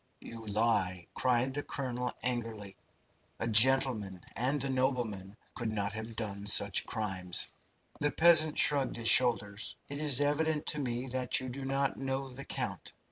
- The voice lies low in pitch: Yes, low, 125 Hz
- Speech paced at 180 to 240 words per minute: No, average, 155 wpm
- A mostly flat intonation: No, average, 3.9 semitones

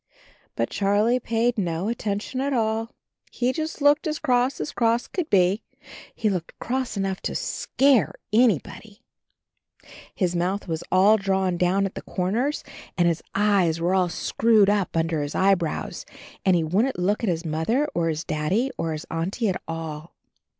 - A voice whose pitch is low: No, high, 195 Hz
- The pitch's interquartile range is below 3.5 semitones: No, average, 5.3 semitones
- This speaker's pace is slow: No, average, 175 wpm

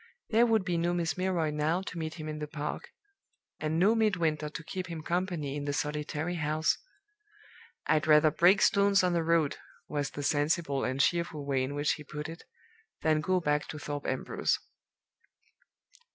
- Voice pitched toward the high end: No, medium, 155 Hz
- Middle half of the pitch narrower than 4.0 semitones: Yes, average, 2.9 semitones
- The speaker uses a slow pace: No, average, 180 wpm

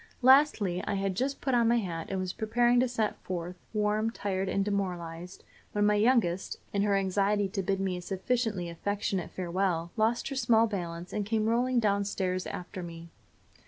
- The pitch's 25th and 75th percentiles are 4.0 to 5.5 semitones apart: No, average, 3.6 semitones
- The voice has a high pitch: Yes, high, 200 Hz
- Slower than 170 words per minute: No, average, 185 wpm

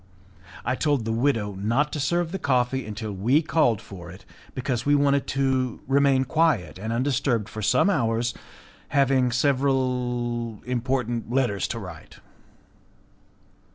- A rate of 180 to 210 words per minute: No, slow, 135 wpm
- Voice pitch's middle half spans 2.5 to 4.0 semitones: Yes, average, 3.5 semitones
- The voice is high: No, low, 125 Hz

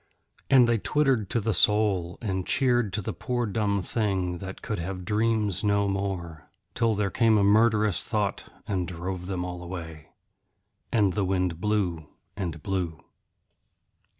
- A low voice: Yes, low, 100 Hz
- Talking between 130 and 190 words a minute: Yes, average, 150 wpm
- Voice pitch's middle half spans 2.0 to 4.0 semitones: Yes, average, 3.1 semitones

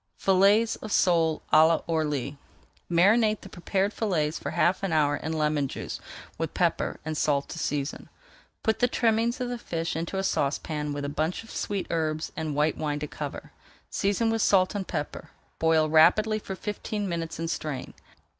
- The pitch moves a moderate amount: Yes, average, 4.8 semitones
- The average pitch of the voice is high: No, medium, 165 Hz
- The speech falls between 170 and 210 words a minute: Yes, average, 175 wpm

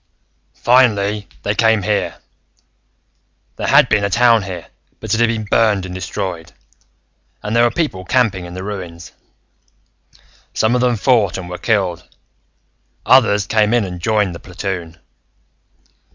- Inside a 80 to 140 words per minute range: No, average, 150 wpm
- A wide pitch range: No, average, 3.7 semitones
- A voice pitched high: No, low, 105 Hz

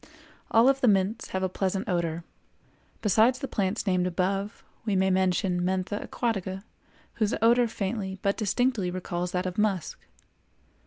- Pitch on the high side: Yes, high, 195 Hz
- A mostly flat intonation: No, average, 3.0 semitones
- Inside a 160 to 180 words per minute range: No, average, 150 wpm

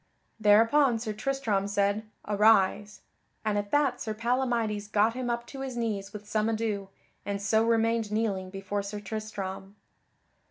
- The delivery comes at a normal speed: Yes, average, 150 wpm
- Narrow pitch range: Yes, narrow, 2.1 semitones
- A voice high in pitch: Yes, high, 215 Hz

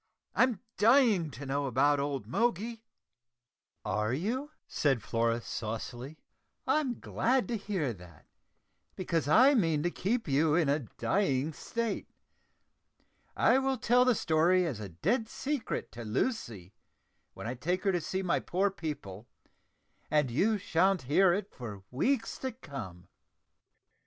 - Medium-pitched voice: Yes, medium, 165 Hz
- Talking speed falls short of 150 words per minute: Yes, average, 140 wpm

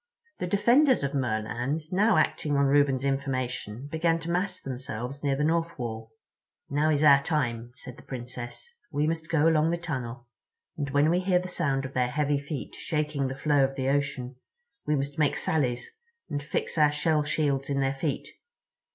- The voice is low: No, medium, 145 Hz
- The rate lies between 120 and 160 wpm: No, average, 180 wpm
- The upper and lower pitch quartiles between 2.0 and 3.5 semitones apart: Yes, average, 3.1 semitones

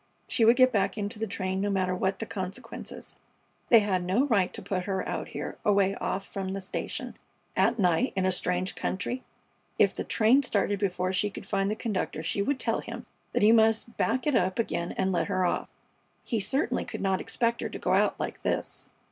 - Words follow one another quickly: Yes, fast, 215 wpm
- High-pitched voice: Yes, high, 200 Hz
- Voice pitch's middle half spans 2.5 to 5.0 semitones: Yes, average, 3.1 semitones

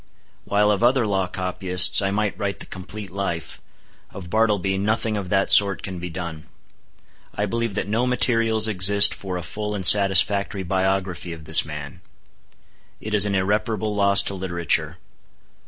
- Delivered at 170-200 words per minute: No, average, 160 wpm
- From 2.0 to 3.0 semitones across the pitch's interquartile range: Yes, narrow, 2.4 semitones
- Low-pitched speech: Yes, low, 100 Hz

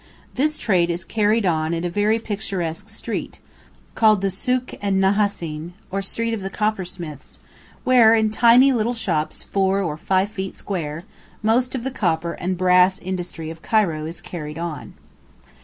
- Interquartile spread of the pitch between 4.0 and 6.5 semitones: Yes, average, 4.4 semitones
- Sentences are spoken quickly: No, average, 160 wpm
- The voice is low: No, high, 190 Hz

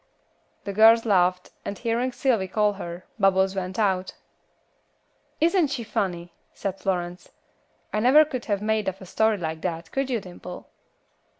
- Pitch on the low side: No, high, 200 Hz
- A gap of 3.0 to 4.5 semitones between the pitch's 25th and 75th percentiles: Yes, average, 3.8 semitones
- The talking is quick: No, average, 155 wpm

